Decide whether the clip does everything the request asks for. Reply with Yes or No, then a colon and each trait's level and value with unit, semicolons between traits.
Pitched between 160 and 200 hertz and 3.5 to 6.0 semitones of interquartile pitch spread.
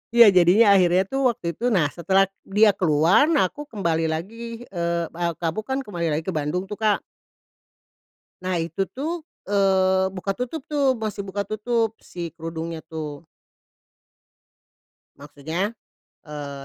Yes: medium, 185 Hz; average, 4.2 semitones